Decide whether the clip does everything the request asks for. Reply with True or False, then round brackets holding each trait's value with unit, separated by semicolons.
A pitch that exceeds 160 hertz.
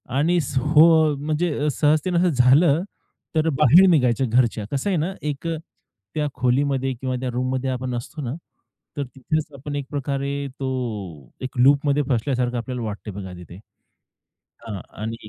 False (135 Hz)